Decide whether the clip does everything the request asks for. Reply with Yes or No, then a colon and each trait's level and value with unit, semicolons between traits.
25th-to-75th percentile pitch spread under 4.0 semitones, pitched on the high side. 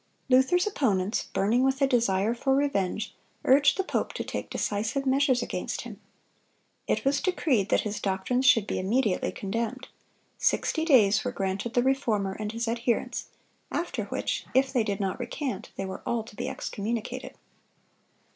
No: average, 4.5 semitones; high, 235 Hz